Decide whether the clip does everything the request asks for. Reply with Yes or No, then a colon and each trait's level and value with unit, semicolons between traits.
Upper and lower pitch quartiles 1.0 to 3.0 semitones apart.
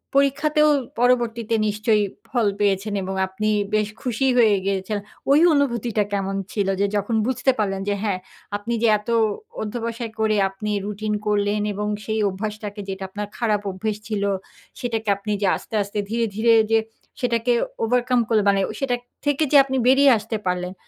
Yes: narrow, 2.6 semitones